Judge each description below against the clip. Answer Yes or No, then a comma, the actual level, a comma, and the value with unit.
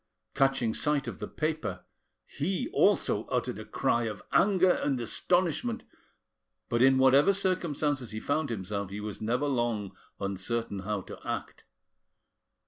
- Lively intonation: Yes, wide, 6.2 semitones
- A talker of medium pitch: No, low, 130 Hz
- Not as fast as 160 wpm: Yes, slow, 135 wpm